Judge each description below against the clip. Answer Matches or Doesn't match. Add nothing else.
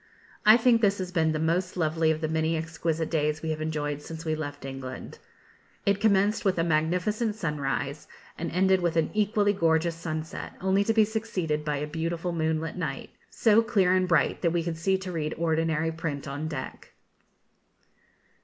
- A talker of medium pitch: Matches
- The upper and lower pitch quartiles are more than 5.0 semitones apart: Doesn't match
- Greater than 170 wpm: Matches